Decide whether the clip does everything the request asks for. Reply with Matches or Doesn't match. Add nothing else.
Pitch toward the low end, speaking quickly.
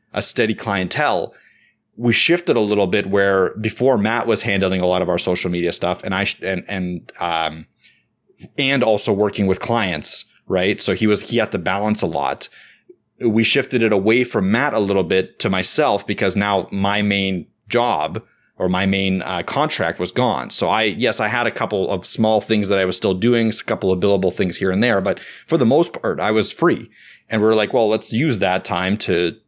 Matches